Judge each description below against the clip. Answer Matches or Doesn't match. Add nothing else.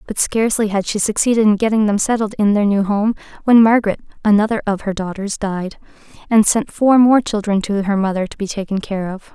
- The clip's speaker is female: Matches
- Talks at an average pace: Doesn't match